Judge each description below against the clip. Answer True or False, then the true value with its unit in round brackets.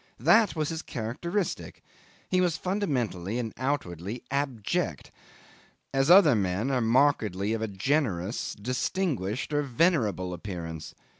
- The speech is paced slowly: True (120 wpm)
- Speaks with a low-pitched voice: True (125 Hz)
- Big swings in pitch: True (7.1 semitones)